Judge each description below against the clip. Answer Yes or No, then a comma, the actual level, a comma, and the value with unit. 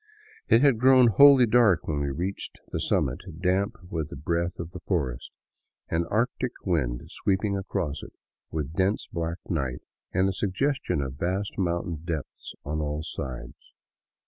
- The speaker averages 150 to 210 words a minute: Yes, average, 155 wpm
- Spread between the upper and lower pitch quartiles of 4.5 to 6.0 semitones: Yes, average, 4.8 semitones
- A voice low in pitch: Yes, very low, 85 Hz